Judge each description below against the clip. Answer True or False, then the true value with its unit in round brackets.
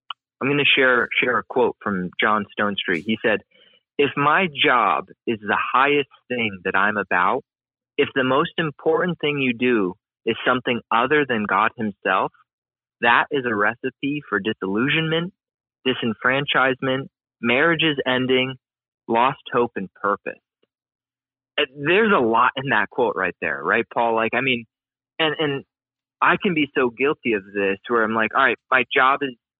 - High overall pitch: False (130 Hz)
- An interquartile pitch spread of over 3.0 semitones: True (3.8 semitones)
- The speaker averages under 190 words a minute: True (160 wpm)